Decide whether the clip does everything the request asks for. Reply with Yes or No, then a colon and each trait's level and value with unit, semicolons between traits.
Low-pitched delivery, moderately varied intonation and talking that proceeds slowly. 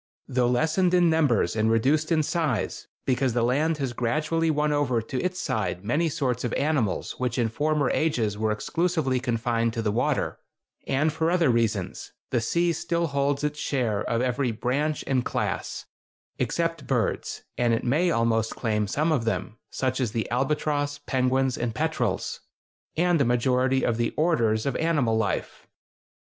No: low, 130 Hz; average, 4.9 semitones; average, 165 wpm